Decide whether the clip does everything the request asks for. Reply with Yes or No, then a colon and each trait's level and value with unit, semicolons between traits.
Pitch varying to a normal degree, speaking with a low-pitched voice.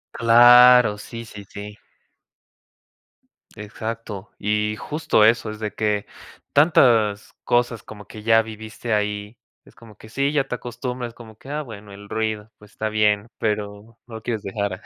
No: narrow, 2.2 semitones; low, 110 Hz